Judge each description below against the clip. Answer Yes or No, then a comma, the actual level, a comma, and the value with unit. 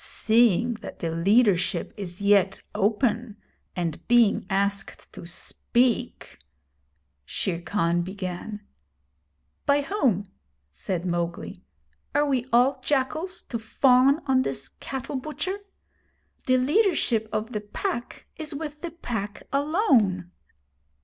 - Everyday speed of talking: No, slow, 115 wpm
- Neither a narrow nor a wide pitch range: No, wide, 6.2 semitones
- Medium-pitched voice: No, high, 225 Hz